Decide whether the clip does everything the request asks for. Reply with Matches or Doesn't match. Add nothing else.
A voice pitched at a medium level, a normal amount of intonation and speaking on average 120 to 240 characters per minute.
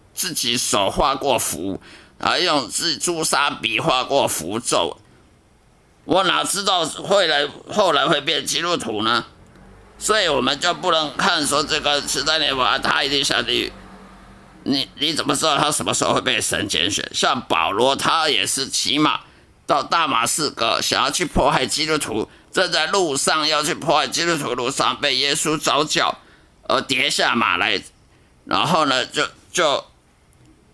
Matches